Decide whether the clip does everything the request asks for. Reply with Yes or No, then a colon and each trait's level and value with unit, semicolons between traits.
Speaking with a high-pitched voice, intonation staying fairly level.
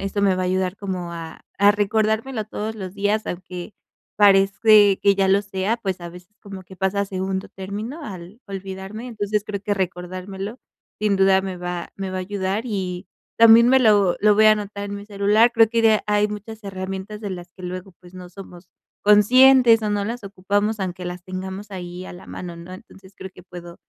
Yes: high, 195 Hz; narrow, 2.1 semitones